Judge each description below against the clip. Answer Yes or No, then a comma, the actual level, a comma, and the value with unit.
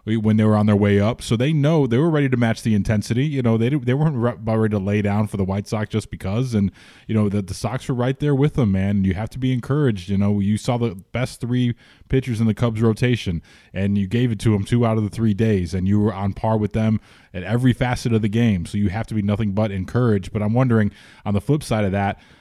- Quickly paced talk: Yes, fast, 275 wpm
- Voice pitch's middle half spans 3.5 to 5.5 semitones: No, average, 3.1 semitones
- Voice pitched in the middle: No, low, 110 Hz